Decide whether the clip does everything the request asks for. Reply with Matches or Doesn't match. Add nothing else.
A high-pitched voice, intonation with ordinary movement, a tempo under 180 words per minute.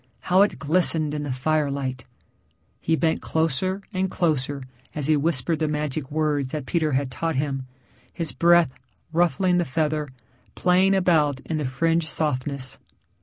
Doesn't match